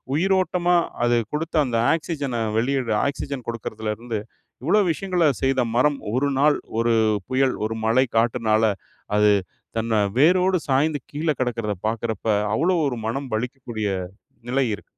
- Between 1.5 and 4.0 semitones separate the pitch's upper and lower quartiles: No, average, 4.6 semitones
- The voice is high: No, low, 130 Hz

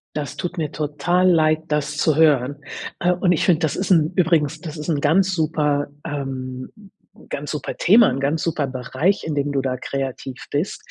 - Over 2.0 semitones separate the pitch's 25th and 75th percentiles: Yes, average, 2.9 semitones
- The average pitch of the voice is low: No, medium, 150 Hz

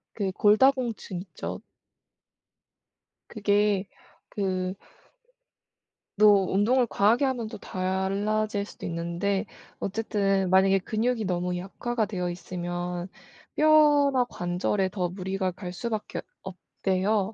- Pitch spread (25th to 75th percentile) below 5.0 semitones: Yes, average, 2.8 semitones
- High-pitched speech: Yes, high, 195 Hz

